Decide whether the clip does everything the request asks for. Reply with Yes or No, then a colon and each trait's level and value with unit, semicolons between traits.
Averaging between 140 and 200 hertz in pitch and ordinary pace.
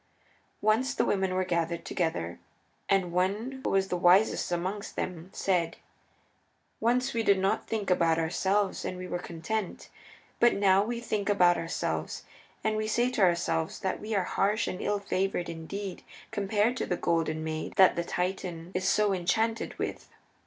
Yes: high, 190 Hz; average, 165 wpm